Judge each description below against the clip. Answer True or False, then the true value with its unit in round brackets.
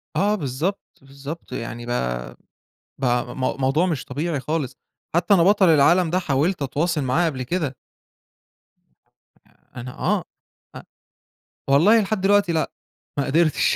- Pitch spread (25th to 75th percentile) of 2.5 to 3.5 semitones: False (5.1 semitones)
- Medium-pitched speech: True (150 Hz)